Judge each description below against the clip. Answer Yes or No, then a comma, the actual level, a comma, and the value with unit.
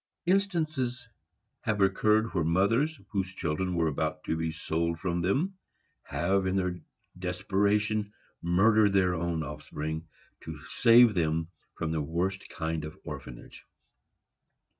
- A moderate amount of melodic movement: Yes, average, 4.7 semitones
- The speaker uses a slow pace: Yes, slow, 125 wpm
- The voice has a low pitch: Yes, very low, 95 Hz